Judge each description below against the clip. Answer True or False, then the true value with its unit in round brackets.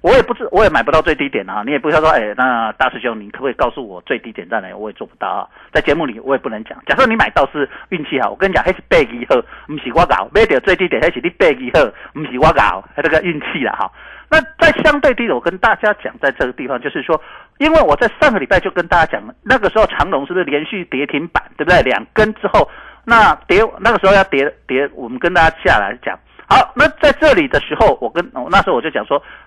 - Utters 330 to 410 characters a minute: True (370 characters per minute)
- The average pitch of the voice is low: False (215 Hz)